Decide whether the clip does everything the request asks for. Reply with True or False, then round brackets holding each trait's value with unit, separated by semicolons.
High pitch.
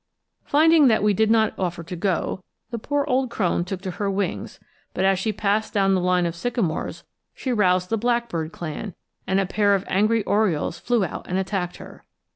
True (200 Hz)